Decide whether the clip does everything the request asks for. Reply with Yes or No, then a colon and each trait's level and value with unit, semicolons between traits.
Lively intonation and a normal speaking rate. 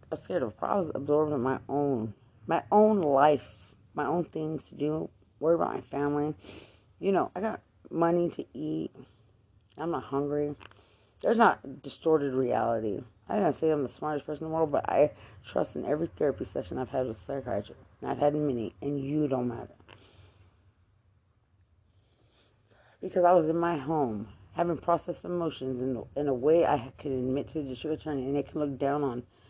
Yes: wide, 6.2 semitones; average, 185 wpm